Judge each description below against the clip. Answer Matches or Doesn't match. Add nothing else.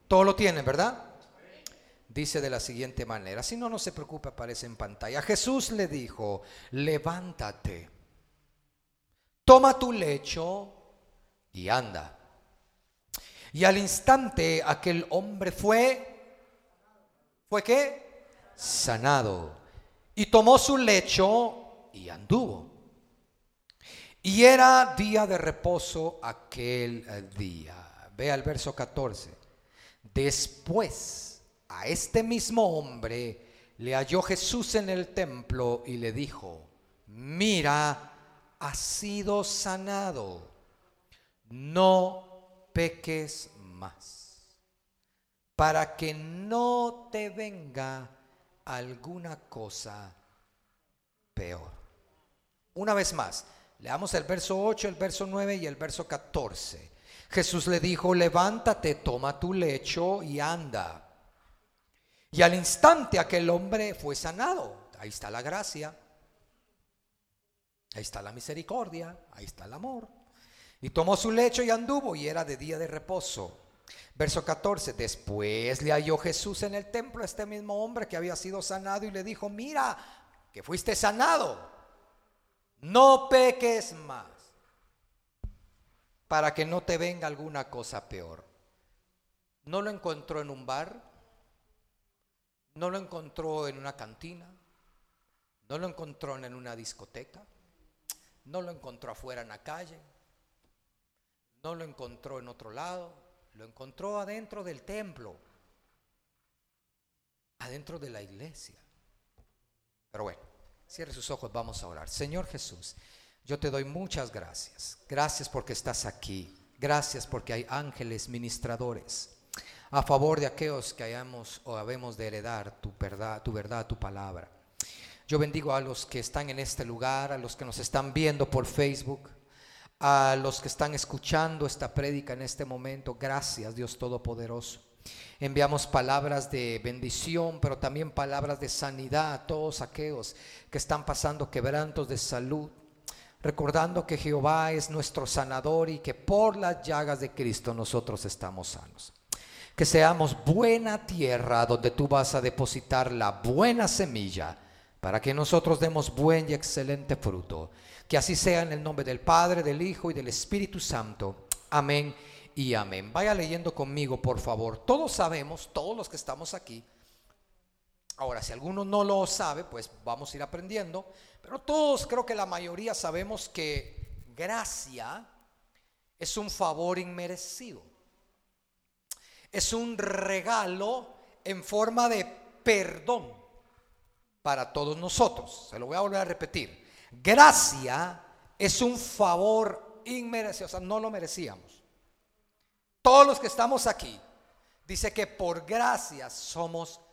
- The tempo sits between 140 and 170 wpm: Doesn't match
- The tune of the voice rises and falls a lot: Matches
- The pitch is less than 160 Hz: Matches